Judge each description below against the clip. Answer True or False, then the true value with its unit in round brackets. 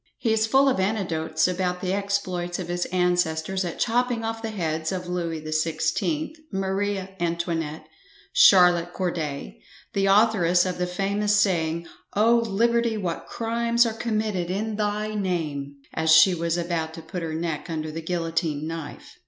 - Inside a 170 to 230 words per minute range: False (160 wpm)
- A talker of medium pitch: True (180 Hz)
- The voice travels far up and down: False (4.2 semitones)